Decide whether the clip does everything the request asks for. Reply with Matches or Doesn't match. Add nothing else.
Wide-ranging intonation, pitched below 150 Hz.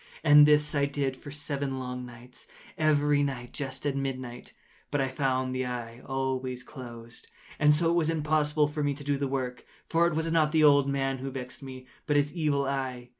Doesn't match